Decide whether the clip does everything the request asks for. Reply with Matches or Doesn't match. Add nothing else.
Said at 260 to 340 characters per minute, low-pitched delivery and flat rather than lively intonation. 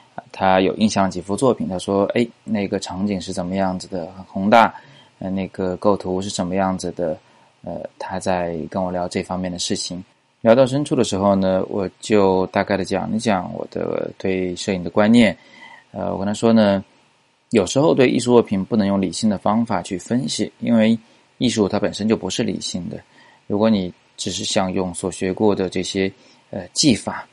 Matches